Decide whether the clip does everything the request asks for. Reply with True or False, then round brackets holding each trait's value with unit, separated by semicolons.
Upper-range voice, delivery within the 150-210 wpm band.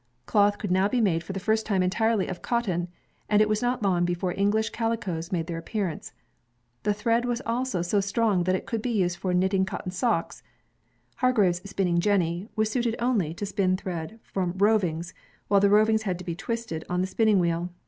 True (195 Hz; 200 wpm)